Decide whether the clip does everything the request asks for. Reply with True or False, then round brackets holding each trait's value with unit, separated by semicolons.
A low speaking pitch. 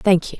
False (185 Hz)